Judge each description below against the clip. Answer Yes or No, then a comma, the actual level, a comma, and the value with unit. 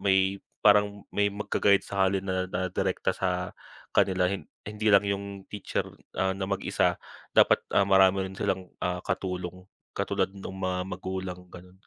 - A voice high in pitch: No, very low, 95 Hz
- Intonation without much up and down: Yes, narrow, 1.2 semitones